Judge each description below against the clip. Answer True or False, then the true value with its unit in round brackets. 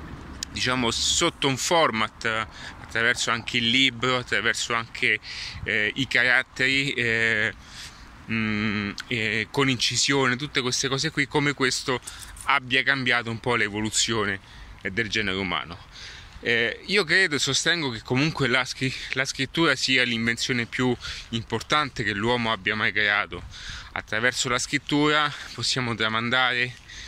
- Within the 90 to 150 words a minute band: True (130 wpm)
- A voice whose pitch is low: True (120 Hz)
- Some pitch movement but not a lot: True (3.4 semitones)